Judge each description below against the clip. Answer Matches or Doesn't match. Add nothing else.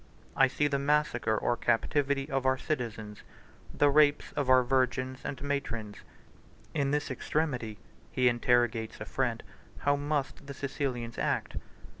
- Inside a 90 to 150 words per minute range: Matches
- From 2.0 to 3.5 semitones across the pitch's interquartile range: Matches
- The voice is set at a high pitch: Doesn't match